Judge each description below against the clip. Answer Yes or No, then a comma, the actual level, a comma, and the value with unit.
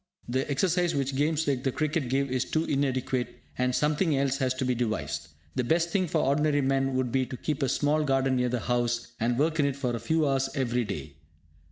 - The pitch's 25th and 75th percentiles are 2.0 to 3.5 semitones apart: Yes, average, 3.0 semitones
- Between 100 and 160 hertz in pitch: Yes, low, 135 Hz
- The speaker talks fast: Yes, fast, 225 wpm